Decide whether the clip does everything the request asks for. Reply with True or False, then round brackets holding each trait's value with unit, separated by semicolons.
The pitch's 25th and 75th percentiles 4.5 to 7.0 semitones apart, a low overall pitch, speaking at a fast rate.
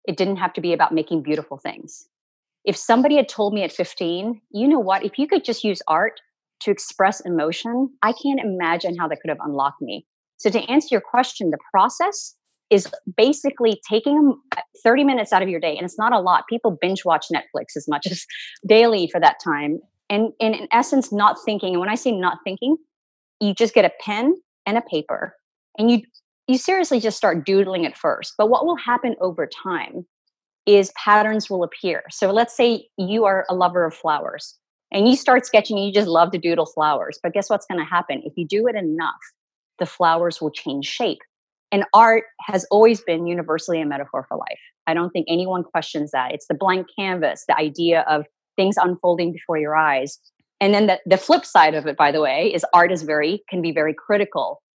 False (5.3 semitones; 195 Hz; 210 wpm)